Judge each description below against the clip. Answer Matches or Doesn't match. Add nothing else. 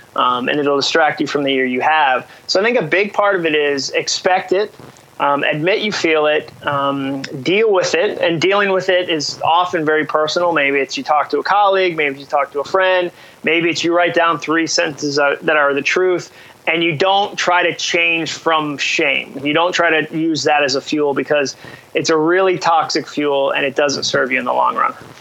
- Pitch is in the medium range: Matches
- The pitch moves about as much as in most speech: Matches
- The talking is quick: Matches